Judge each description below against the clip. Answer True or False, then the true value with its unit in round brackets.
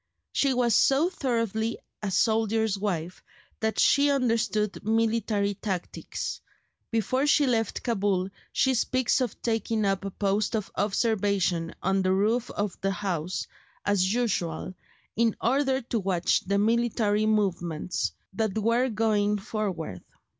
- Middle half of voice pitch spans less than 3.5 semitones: True (3.0 semitones)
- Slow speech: True (130 wpm)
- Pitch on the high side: True (215 Hz)